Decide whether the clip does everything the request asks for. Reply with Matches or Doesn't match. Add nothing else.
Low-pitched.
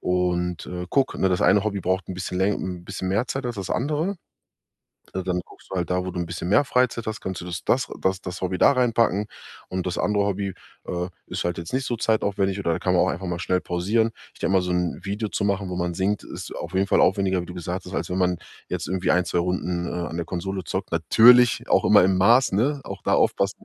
Matches